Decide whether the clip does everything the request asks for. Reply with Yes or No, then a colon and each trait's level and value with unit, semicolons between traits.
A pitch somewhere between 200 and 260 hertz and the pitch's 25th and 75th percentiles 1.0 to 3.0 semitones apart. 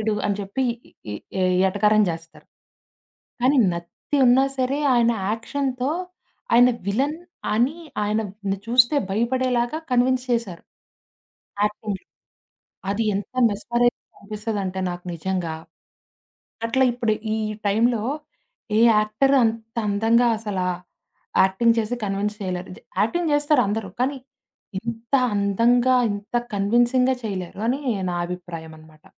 No: high, 220 Hz; average, 3.7 semitones